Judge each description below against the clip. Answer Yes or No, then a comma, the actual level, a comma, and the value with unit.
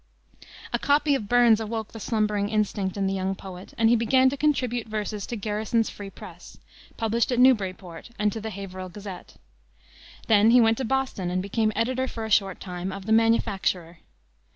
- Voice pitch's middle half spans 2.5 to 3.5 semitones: Yes, average, 3.1 semitones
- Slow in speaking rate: No, average, 185 wpm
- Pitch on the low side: No, high, 215 Hz